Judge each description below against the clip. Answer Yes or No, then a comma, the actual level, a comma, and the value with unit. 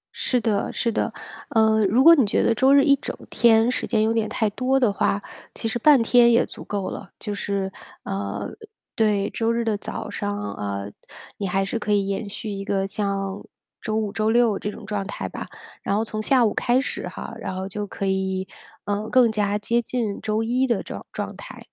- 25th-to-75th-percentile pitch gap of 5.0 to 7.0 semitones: No, average, 2.8 semitones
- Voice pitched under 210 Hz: No, high, 215 Hz